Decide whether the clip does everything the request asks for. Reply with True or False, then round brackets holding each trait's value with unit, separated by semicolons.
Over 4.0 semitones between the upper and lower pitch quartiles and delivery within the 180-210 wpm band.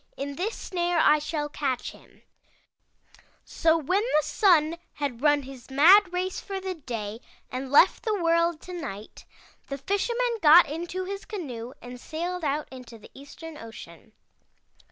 False (5.2 semitones; 155 wpm)